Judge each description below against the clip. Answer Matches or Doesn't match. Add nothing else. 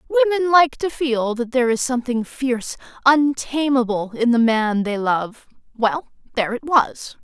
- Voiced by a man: Doesn't match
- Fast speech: Doesn't match